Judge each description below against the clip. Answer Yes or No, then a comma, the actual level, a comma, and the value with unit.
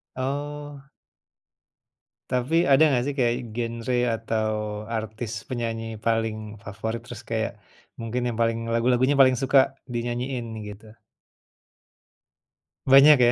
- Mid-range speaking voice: No, low, 120 Hz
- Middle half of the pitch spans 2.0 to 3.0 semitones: Yes, average, 2.7 semitones